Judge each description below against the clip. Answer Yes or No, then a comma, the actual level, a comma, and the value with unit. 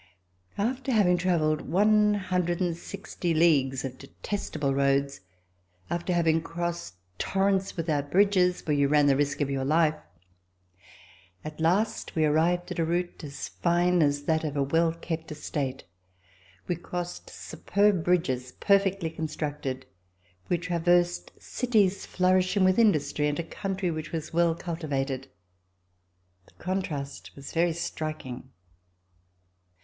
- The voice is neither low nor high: Yes, medium, 165 Hz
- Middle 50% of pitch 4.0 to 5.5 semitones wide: No, average, 3.6 semitones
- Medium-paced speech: No, slow, 130 wpm